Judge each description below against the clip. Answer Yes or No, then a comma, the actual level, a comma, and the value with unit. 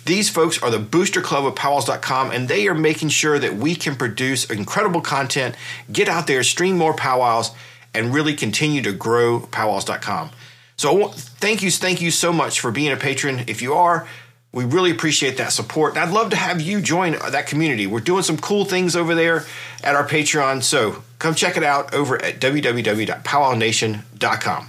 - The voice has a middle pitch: Yes, medium, 150 Hz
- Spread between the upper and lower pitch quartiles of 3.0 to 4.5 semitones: No, average, 5.1 semitones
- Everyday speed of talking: Yes, average, 185 wpm